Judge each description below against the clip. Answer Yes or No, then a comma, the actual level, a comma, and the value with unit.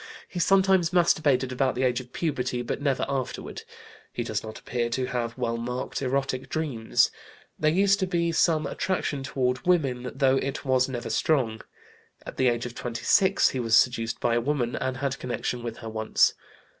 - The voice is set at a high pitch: No, low, 130 Hz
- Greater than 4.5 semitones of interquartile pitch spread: No, average, 3.7 semitones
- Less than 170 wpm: No, average, 180 wpm